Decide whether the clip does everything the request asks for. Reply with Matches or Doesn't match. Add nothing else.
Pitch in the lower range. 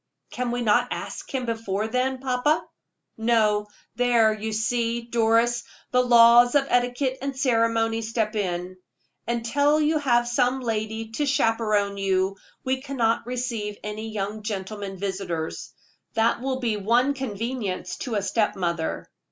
Doesn't match